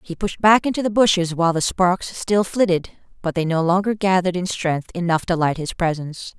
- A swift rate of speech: Yes, fast, 215 wpm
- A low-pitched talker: No, medium, 180 Hz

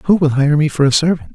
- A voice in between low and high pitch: Yes, medium, 150 Hz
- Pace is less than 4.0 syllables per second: No, 6.1 syllables/s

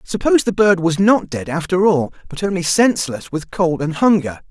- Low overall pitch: No, medium, 180 Hz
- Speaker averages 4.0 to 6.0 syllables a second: Yes, 5.3 syllables/s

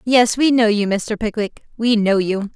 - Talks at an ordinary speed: No, fast, 210 wpm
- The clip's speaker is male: No, female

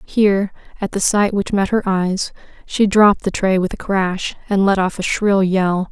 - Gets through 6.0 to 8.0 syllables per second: No, 4.6 syllables/s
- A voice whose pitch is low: No, high, 195 Hz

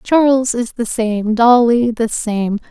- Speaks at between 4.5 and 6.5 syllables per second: No, 3.6 syllables/s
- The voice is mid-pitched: No, high, 235 Hz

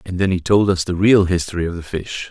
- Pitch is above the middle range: No, very low, 90 Hz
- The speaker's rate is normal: No, fast, 285 wpm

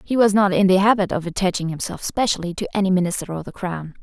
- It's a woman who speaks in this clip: Yes, female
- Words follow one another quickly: Yes, fast, 240 wpm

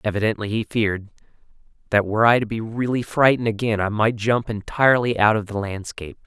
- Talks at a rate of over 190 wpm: No, average, 180 wpm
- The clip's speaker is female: No, male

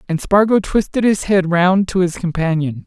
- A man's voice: Yes, male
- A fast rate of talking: No, average, 190 wpm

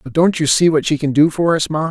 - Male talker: Yes, male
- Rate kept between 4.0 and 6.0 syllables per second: Yes, 5.7 syllables/s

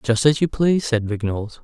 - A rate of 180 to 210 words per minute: No, fast, 220 wpm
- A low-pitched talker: Yes, low, 125 Hz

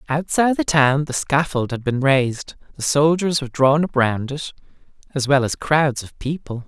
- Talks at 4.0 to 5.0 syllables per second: Yes, 4.9 syllables/s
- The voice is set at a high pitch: No, medium, 140 Hz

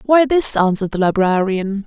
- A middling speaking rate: Yes, average, 160 wpm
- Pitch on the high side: Yes, high, 215 Hz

